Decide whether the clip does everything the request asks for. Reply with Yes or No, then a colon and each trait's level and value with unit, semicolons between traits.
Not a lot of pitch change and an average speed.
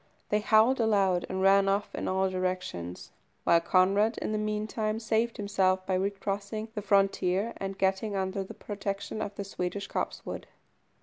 Yes: narrow, 2.1 semitones; average, 160 wpm